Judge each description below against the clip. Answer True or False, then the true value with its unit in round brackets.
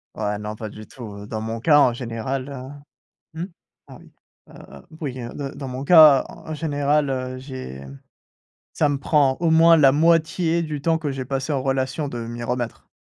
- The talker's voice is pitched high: False (135 Hz)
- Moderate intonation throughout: True (3.7 semitones)